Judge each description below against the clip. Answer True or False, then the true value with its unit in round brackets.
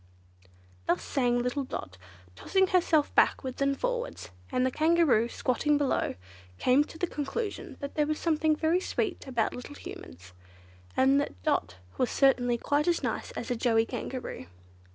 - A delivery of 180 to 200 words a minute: False (155 wpm)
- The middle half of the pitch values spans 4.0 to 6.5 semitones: True (4.4 semitones)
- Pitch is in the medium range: False (275 Hz)